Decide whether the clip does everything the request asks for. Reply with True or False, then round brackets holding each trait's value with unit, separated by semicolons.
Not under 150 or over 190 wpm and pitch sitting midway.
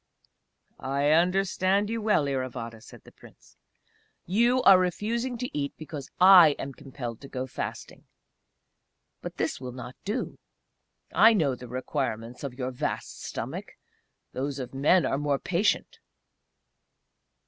False (135 wpm; 145 Hz)